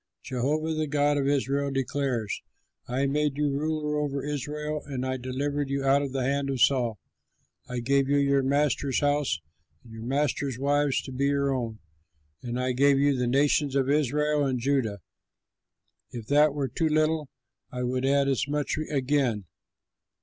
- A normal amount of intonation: No, narrow, 2.0 semitones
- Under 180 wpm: Yes, average, 170 wpm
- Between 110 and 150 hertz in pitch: Yes, medium, 140 Hz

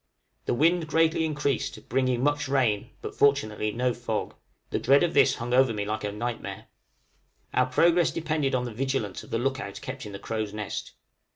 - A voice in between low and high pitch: No, low, 130 Hz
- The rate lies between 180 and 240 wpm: Yes, average, 190 wpm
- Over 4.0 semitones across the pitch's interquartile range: Yes, average, 4.4 semitones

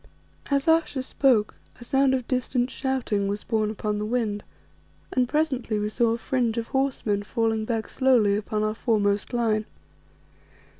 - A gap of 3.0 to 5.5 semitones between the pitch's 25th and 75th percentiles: Yes, average, 3.5 semitones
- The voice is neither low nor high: No, high, 230 Hz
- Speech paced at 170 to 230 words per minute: No, average, 155 wpm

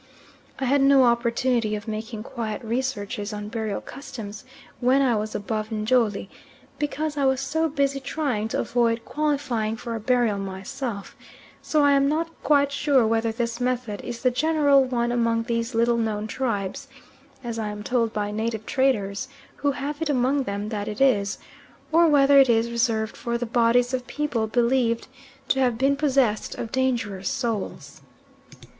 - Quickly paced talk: No, average, 165 wpm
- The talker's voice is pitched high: Yes, high, 235 Hz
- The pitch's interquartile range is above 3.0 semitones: Yes, average, 3.7 semitones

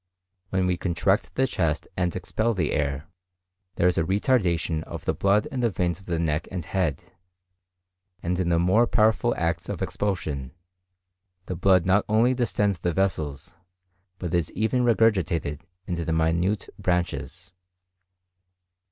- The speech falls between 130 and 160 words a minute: Yes, average, 150 wpm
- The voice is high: No, very low, 90 Hz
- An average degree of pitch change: Yes, average, 3.5 semitones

